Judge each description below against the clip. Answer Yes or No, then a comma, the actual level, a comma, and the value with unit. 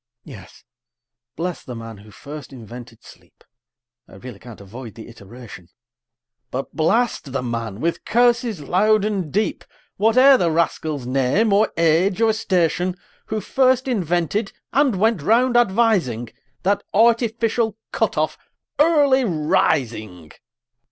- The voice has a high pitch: No, medium, 180 Hz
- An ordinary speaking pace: No, slow, 125 wpm